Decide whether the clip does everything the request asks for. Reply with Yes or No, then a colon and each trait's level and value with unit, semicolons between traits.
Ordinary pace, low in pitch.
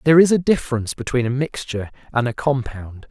Yes: average, 195 wpm; low, 130 Hz